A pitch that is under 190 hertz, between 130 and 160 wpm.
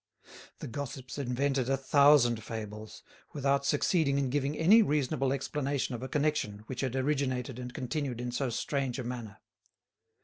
Yes: low, 135 Hz; average, 150 wpm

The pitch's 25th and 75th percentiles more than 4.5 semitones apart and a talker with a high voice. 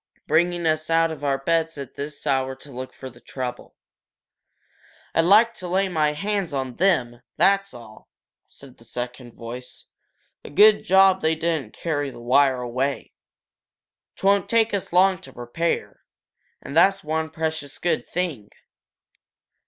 No: average, 5.3 semitones; medium, 155 Hz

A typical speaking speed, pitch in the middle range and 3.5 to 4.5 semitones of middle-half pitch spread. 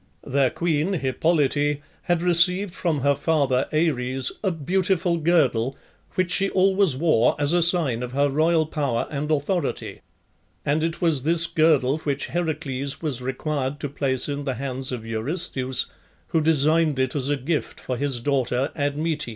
Yes: average, 160 wpm; medium, 145 Hz; average, 3.8 semitones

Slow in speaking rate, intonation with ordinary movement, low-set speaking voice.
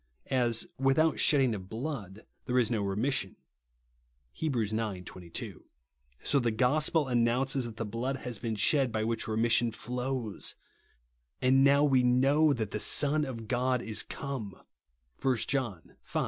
No: average, 160 wpm; average, 3.7 semitones; low, 120 Hz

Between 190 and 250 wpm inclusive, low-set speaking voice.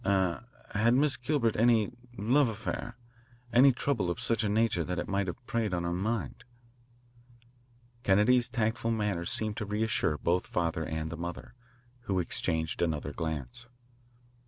No: average, 160 wpm; low, 105 Hz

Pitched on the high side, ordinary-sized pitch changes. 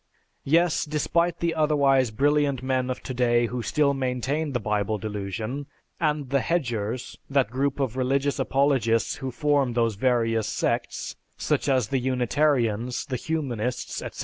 No: low, 130 Hz; average, 3.2 semitones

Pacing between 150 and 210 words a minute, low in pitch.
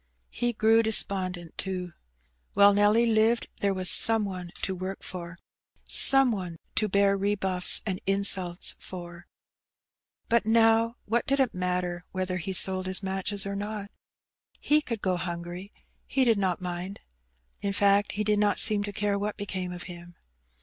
No: average, 160 wpm; high, 195 Hz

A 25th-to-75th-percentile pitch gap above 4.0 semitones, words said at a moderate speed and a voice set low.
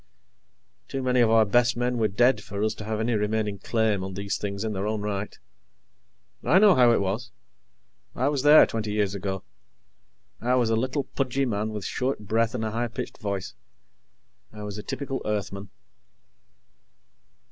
No: average, 3.1 semitones; average, 180 wpm; low, 110 Hz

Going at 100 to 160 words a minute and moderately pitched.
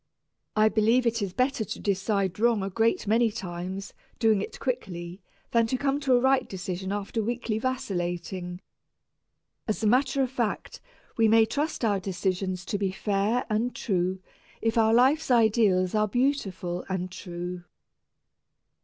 No: average, 155 wpm; high, 215 Hz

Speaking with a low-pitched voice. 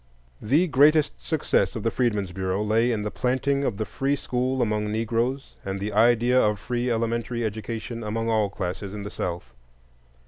Yes: low, 115 Hz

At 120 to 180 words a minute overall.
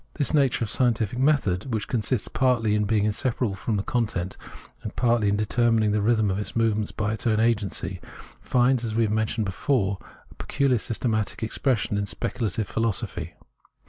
Yes: average, 175 wpm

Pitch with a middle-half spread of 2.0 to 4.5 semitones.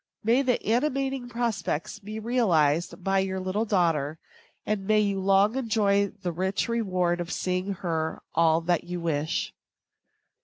Yes: average, 4.1 semitones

